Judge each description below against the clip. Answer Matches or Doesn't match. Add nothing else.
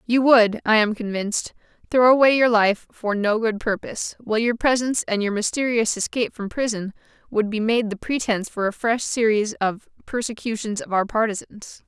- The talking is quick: Doesn't match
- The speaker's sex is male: Doesn't match